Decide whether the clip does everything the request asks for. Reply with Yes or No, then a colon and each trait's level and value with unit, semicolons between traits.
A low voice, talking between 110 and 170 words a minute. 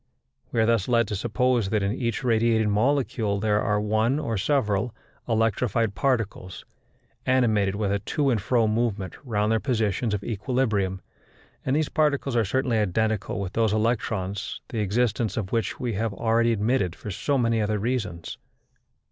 Yes: low, 110 Hz; average, 165 wpm